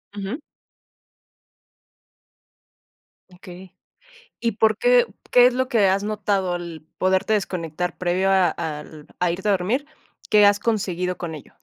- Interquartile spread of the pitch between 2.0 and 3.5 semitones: Yes, average, 3.2 semitones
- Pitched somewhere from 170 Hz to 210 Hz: Yes, high, 190 Hz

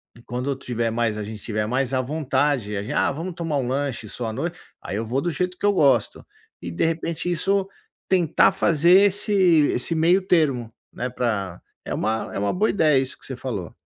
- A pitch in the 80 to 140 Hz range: Yes, low, 135 Hz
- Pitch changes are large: Yes, wide, 6.5 semitones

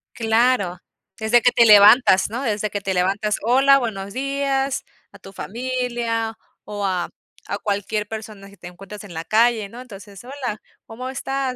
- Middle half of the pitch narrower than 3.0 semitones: No, average, 3.8 semitones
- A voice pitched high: Yes, high, 220 Hz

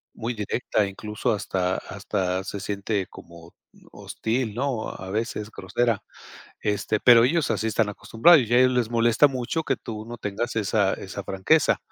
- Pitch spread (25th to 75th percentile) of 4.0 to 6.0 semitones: No, average, 3.2 semitones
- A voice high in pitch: No, low, 110 Hz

